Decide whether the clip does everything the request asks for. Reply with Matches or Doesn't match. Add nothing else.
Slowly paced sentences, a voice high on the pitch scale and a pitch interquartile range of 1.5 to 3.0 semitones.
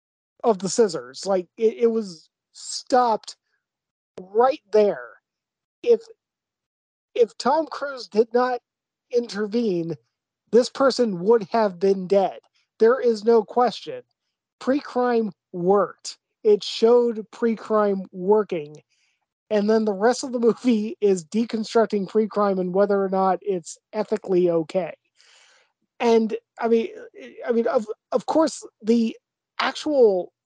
Doesn't match